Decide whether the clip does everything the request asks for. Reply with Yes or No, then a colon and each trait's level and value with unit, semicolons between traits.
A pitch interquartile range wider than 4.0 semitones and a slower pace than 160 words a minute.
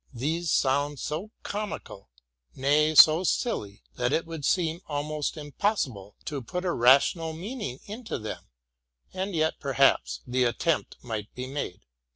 Yes: average, 4.7 semitones; average, 140 wpm